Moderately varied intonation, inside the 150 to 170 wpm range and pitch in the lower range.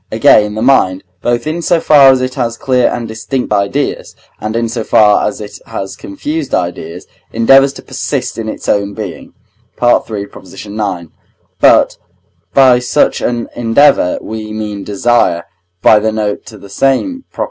Yes: average, 3.9 semitones; average, 160 wpm; low, 115 Hz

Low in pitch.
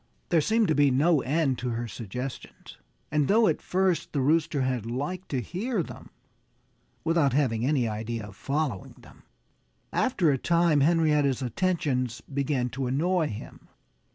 No: medium, 145 Hz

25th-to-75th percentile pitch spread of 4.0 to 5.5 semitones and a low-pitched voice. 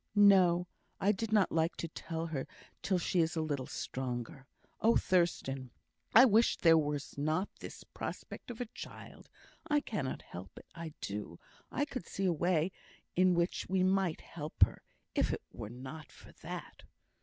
No: average, 4.7 semitones; medium, 170 Hz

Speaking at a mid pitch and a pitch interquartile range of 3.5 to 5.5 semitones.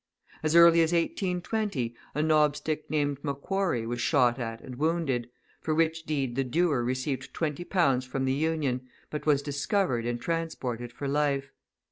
Yes: medium, 145 Hz; average, 4.1 semitones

